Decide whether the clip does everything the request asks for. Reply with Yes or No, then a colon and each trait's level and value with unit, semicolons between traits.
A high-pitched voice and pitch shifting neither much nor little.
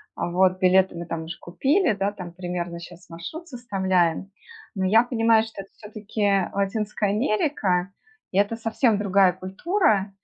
Yes: high, 195 Hz; average, 3.3 semitones